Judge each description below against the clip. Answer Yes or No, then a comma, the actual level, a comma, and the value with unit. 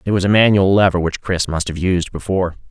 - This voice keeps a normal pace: No, fast, 245 wpm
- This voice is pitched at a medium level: No, very low, 95 Hz